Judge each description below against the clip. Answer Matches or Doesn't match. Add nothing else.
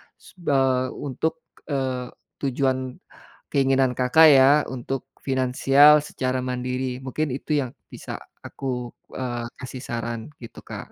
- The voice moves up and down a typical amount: Doesn't match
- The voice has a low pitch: Matches